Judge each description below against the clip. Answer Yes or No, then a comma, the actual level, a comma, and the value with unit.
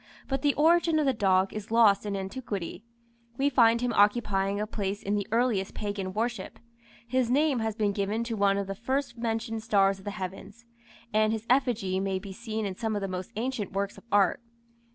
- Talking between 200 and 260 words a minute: Yes, fast, 205 wpm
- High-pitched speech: Yes, high, 215 Hz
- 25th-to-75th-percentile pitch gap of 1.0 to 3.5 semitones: Yes, average, 3.1 semitones